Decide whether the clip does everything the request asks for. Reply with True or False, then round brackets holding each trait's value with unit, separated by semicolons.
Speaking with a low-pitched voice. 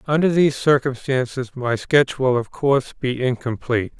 True (130 Hz)